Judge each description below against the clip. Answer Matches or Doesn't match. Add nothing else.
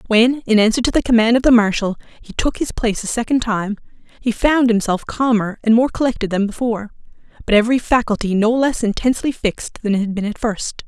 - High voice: Matches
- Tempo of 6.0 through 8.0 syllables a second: Matches